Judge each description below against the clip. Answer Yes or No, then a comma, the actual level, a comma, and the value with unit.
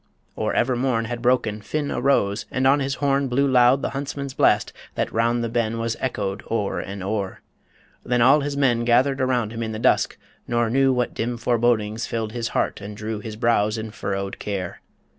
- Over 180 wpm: Yes, average, 200 wpm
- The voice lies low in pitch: Yes, low, 120 Hz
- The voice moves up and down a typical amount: Yes, average, 3.1 semitones